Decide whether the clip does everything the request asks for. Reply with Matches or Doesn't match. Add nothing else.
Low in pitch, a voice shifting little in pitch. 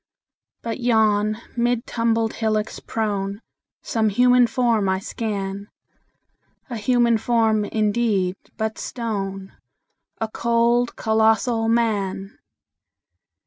Doesn't match